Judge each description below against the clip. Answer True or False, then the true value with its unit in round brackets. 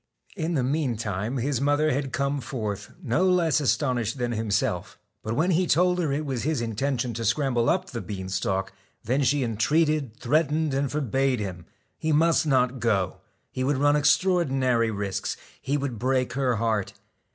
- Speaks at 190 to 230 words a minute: False (175 wpm)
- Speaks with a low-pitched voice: True (130 Hz)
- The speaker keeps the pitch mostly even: False (4.5 semitones)